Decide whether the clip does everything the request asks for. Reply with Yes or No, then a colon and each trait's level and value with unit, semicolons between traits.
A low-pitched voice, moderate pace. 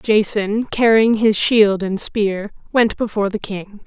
No: high, 210 Hz; average, 155 wpm